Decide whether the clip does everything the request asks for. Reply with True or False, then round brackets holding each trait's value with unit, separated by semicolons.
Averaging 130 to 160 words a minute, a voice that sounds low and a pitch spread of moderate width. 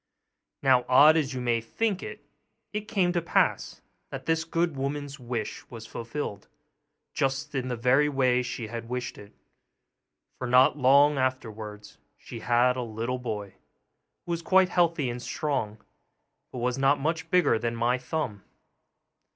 True (155 wpm; 130 Hz; 3.9 semitones)